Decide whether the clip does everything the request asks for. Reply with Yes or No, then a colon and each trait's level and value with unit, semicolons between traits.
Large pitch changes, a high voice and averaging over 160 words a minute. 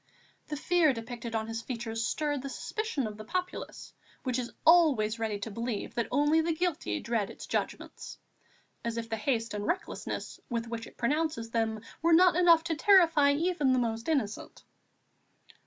Yes: wide, 6.1 semitones; very high, 250 Hz; average, 170 wpm